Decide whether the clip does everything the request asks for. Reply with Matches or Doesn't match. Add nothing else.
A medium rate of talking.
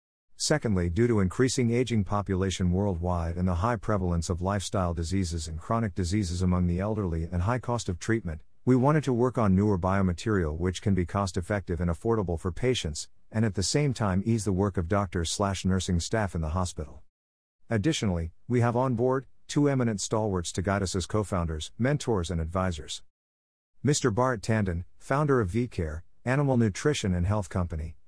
Matches